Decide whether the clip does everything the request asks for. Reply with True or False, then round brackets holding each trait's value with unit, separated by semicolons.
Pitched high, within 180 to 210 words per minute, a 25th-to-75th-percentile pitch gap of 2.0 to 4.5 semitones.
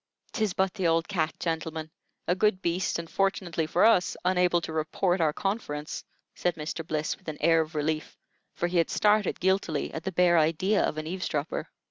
False (170 Hz; 190 wpm; 2.9 semitones)